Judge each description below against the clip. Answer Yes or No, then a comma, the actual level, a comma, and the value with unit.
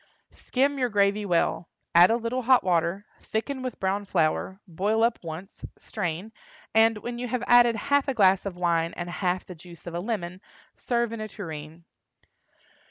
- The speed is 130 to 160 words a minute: No, average, 175 wpm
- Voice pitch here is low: No, high, 200 Hz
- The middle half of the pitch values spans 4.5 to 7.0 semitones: Yes, average, 5.0 semitones